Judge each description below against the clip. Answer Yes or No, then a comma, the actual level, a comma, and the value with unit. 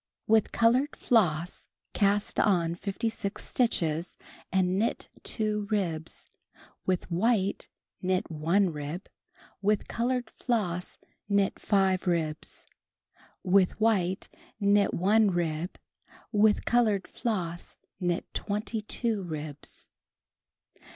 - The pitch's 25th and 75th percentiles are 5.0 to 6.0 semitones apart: No, average, 3.7 semitones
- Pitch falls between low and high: No, high, 195 Hz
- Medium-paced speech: No, slow, 95 wpm